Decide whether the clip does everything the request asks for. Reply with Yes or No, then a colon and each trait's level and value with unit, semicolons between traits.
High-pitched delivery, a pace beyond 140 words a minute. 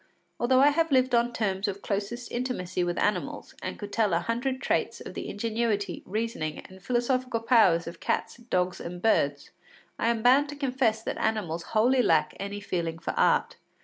Yes: high, 220 Hz; average, 180 wpm